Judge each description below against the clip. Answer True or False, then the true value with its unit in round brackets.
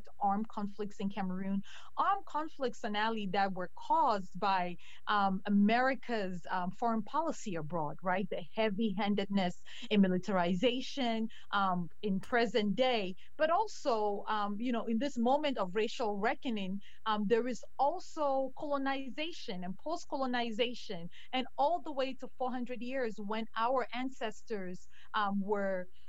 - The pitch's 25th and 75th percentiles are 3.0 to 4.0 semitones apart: False (4.5 semitones)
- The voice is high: True (220 Hz)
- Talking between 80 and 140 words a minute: True (135 wpm)